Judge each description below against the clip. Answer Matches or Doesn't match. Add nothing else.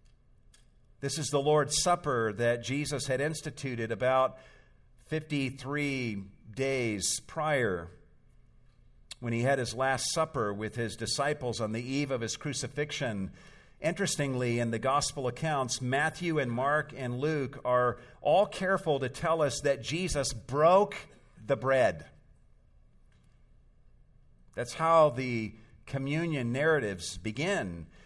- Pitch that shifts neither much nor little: Matches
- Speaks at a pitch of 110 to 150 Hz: Matches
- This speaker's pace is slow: Matches